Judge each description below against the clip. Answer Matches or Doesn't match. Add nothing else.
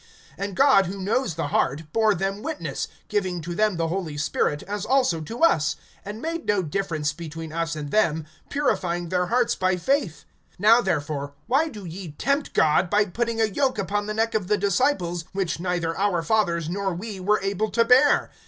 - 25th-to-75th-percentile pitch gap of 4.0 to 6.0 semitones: Matches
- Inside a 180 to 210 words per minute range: Matches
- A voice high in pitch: Matches